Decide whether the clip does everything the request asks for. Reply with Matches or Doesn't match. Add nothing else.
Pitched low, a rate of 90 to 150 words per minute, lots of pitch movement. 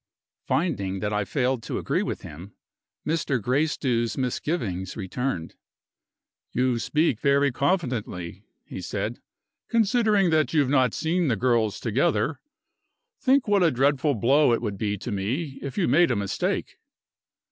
Matches